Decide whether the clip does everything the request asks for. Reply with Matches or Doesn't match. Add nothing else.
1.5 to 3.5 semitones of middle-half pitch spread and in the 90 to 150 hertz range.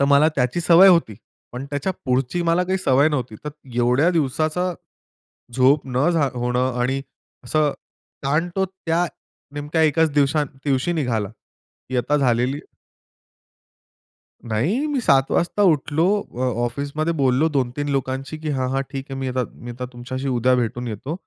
Doesn't match